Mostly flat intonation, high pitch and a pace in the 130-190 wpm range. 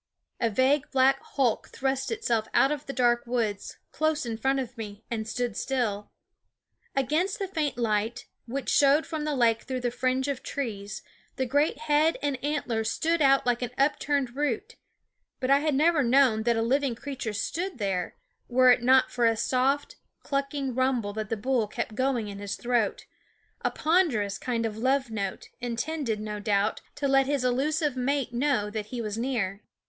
No: average, 3.8 semitones; very high, 255 Hz; average, 180 wpm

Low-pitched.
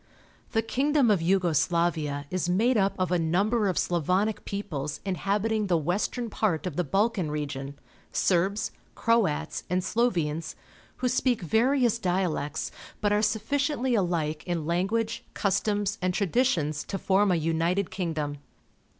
No: high, 190 Hz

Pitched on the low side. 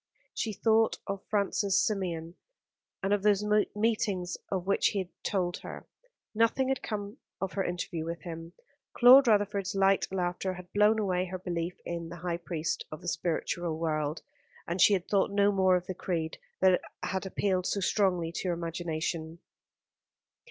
No: medium, 185 Hz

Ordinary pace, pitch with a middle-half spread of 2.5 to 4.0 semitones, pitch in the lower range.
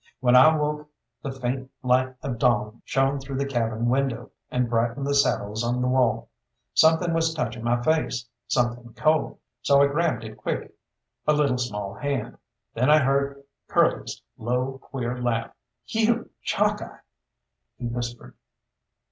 Yes: average, 150 wpm; average, 2.8 semitones; low, 130 Hz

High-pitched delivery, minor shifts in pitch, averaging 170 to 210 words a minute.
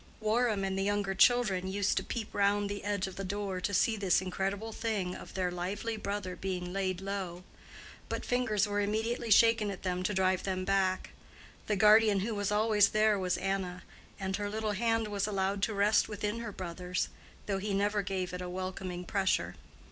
Yes: high, 200 Hz; narrow, 2.0 semitones; average, 195 wpm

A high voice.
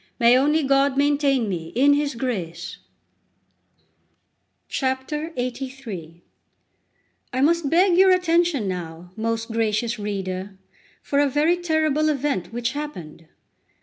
Yes: very high, 260 Hz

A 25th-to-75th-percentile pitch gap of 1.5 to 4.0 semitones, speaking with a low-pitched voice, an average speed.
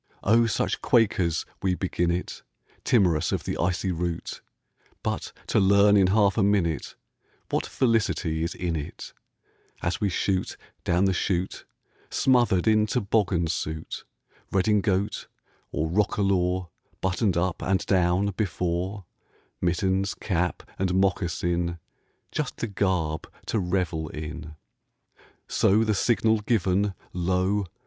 No: average, 2.7 semitones; very low, 95 Hz; slow, 120 wpm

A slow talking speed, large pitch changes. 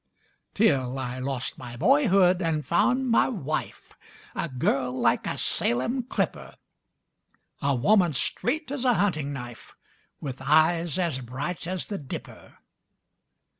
Yes: slow, 130 wpm; wide, 7.2 semitones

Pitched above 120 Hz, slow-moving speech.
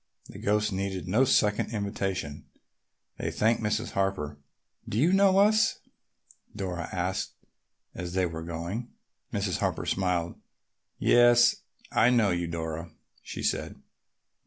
No: very low, 95 Hz; slow, 125 wpm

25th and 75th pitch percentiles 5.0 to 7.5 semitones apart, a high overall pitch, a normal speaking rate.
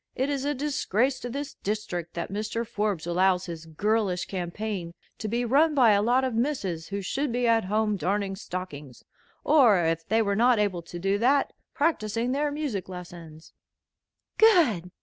Yes: wide, 5.6 semitones; high, 210 Hz; average, 170 wpm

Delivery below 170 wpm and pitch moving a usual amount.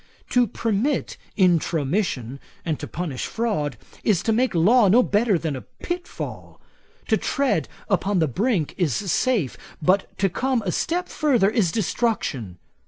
No: average, 145 wpm; wide, 6.6 semitones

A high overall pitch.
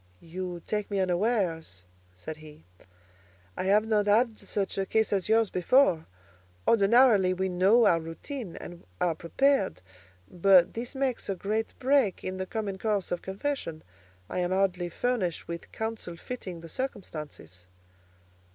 Yes: high, 195 Hz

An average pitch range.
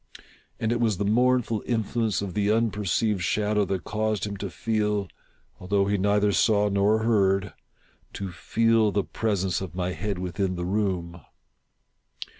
No: narrow, 2.1 semitones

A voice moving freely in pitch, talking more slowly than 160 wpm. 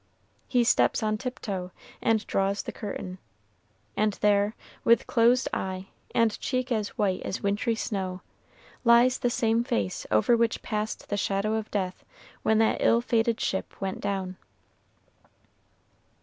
No: average, 3.0 semitones; average, 140 wpm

